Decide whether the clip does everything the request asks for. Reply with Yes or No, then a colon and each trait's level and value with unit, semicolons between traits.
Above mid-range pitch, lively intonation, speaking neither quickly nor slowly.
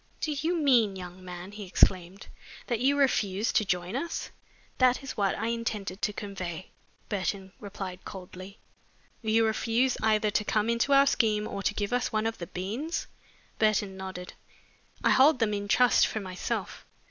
No: high, 210 Hz; average, 3.7 semitones; average, 170 wpm